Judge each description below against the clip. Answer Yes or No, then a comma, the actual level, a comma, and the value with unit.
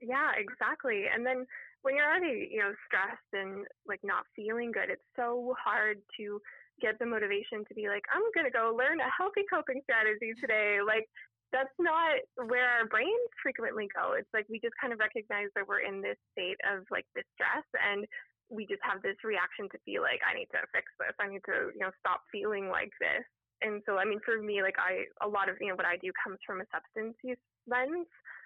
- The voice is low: No, high, 225 Hz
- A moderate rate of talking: No, fast, 215 wpm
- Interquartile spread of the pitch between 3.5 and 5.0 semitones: Yes, average, 4.1 semitones